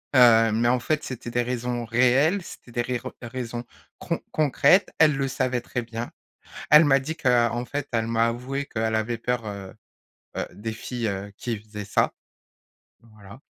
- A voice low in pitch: Yes, low, 120 Hz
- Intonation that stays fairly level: Yes, narrow, 2.3 semitones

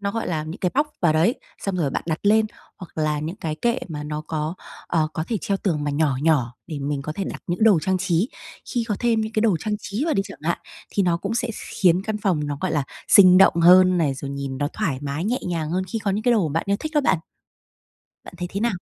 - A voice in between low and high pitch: Yes, medium, 180 Hz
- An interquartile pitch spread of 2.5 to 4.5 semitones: No, average, 5.3 semitones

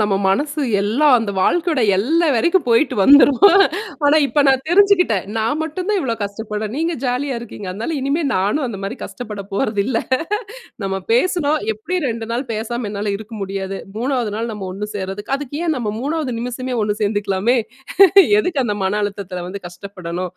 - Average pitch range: No, wide, 6.0 semitones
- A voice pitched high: Yes, high, 230 Hz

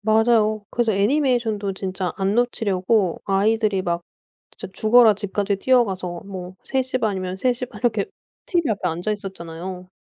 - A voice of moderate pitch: No, high, 205 Hz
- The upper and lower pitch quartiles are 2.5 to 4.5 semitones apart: Yes, average, 3.5 semitones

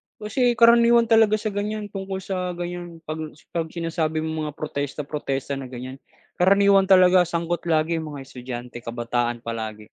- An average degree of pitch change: No, wide, 6.5 semitones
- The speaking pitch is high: No, medium, 165 Hz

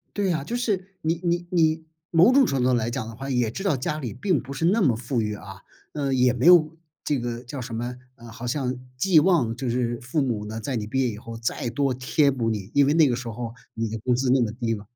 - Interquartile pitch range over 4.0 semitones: Yes, average, 4.8 semitones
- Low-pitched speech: Yes, low, 125 Hz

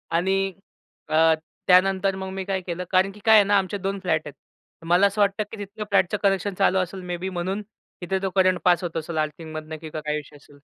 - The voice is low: No, medium, 185 Hz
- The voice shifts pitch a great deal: No, narrow, 2.6 semitones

